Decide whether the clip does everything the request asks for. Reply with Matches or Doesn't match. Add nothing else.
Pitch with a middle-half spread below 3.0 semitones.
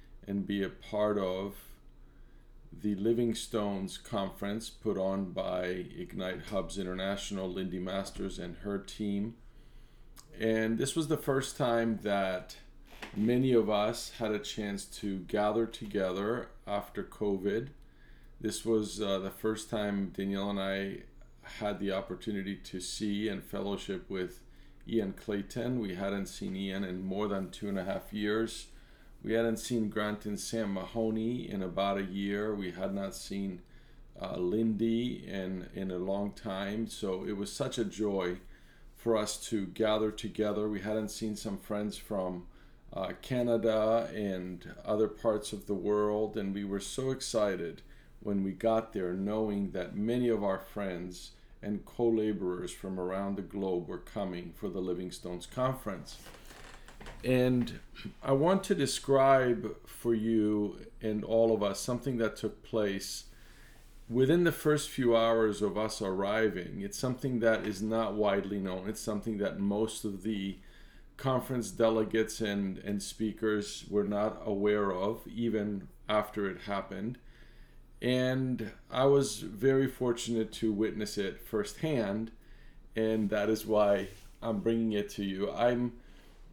Matches